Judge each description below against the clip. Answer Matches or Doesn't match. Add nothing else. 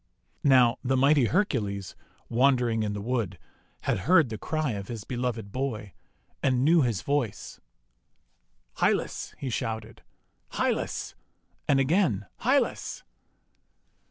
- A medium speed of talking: Doesn't match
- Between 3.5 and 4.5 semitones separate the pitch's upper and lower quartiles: Matches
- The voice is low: Matches